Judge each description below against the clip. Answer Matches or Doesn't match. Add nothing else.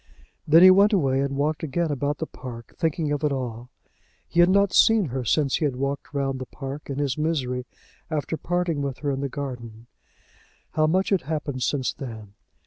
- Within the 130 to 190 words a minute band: Doesn't match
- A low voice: Doesn't match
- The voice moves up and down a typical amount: Matches